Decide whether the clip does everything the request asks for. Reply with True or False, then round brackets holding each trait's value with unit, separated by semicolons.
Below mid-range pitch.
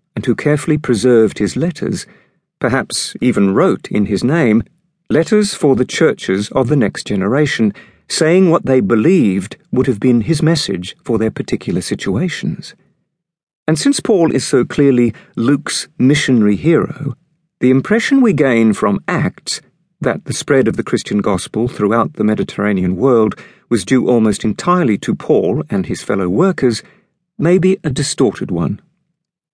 False (145 Hz)